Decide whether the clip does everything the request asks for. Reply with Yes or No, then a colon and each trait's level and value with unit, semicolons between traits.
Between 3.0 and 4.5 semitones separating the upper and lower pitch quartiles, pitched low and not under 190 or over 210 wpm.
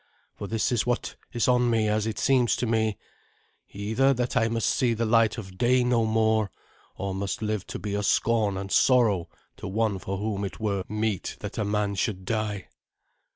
No: narrow, 2.4 semitones; low, 110 Hz; average, 200 wpm